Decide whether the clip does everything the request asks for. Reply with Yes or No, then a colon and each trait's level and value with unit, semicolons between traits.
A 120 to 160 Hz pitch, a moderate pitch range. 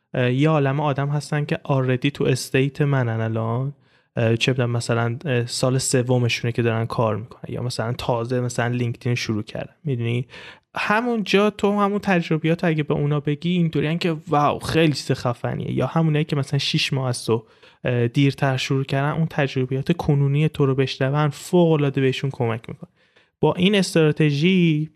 Yes: medium, 140 Hz; average, 3.9 semitones